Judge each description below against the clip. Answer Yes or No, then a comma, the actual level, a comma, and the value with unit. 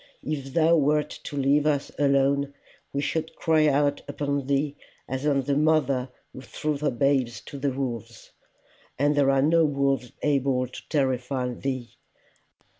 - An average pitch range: No, narrow, 1.8 semitones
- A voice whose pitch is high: No, medium, 140 Hz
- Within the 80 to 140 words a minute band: No, average, 155 wpm